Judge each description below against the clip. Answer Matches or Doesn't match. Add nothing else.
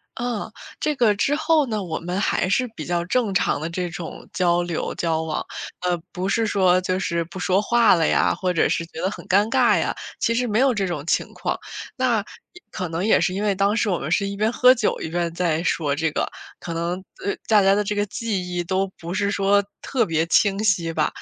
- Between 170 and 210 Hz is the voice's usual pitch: Matches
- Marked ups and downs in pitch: Doesn't match